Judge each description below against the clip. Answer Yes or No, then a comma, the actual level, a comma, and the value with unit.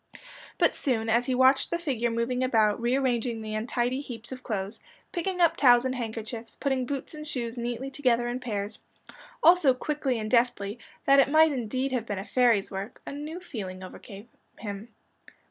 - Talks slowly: No, average, 180 wpm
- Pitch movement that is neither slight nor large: Yes, average, 3.3 semitones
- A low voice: No, high, 245 Hz